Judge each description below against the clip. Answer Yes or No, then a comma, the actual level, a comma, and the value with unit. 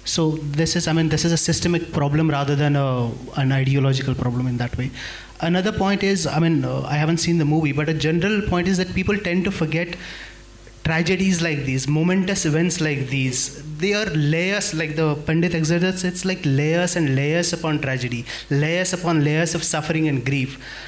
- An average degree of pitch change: Yes, average, 3.8 semitones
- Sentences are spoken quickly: No, average, 195 wpm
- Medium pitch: Yes, medium, 160 Hz